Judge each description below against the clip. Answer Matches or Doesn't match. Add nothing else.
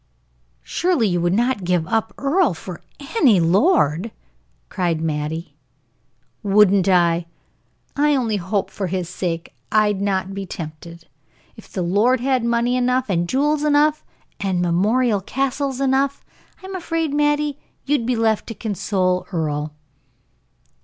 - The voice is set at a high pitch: Matches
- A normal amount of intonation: Doesn't match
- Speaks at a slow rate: Matches